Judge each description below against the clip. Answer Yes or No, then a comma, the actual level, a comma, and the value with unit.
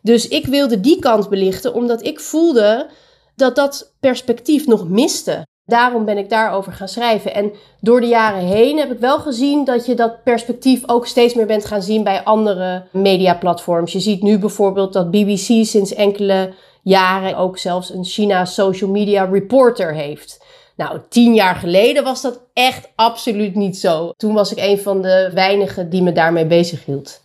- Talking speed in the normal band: Yes, average, 175 wpm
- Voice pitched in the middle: No, high, 210 Hz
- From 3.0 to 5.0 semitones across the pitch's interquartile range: Yes, average, 4.1 semitones